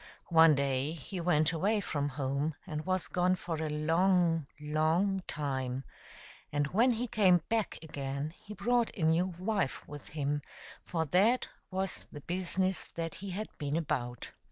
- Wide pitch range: No, average, 4.3 semitones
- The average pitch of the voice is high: No, medium, 165 Hz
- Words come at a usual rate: Yes, average, 155 wpm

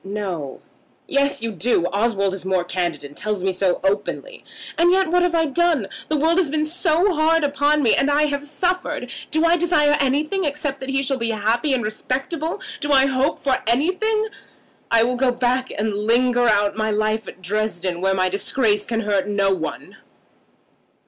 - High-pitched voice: Yes, very high, 255 Hz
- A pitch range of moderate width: No, wide, 6.7 semitones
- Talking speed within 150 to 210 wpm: Yes, average, 185 wpm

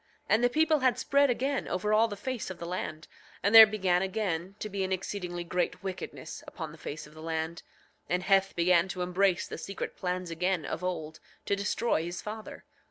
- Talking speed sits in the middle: No, fast, 210 wpm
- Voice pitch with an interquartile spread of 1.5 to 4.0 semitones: Yes, average, 3.6 semitones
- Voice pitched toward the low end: No, medium, 185 Hz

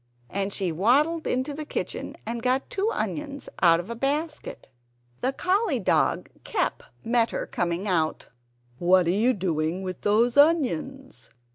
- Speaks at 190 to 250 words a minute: No, average, 150 wpm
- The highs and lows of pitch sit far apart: Yes, wide, 7.5 semitones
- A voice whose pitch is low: No, high, 235 Hz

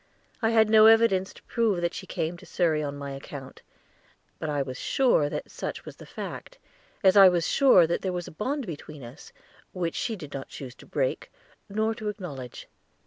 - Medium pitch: Yes, medium, 180 Hz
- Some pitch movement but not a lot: No, wide, 6.9 semitones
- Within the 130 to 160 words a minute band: No, average, 200 wpm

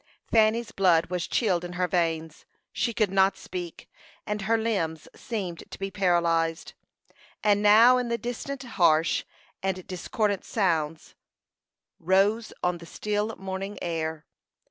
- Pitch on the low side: No, high, 190 Hz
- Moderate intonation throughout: Yes, average, 4.0 semitones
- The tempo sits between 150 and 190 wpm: No, slow, 135 wpm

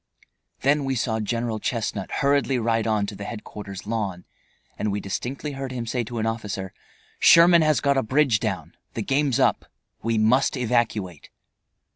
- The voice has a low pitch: Yes, low, 115 Hz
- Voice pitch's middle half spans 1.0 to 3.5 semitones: No, average, 4.1 semitones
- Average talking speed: Yes, average, 165 wpm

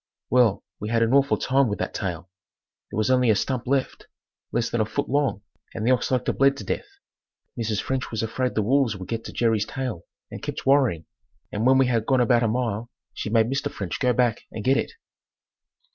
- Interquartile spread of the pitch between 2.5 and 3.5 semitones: Yes, average, 3.1 semitones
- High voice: No, low, 120 Hz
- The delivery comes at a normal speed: No, fast, 220 wpm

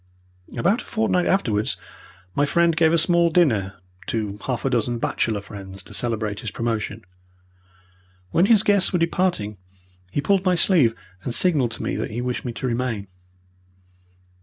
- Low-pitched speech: Yes, low, 125 Hz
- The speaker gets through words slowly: No, average, 160 wpm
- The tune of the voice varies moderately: No, wide, 8.0 semitones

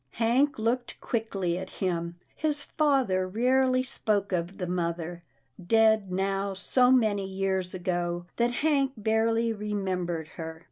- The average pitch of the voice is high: Yes, high, 200 Hz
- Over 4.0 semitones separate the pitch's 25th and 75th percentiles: Yes, average, 4.7 semitones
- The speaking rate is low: Yes, slow, 130 wpm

